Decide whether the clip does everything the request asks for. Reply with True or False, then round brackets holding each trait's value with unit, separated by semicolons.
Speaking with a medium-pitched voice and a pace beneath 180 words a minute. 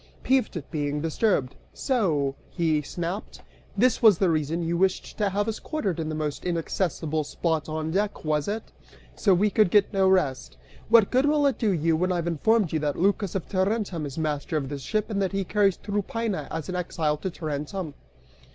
False (180 Hz; 195 wpm)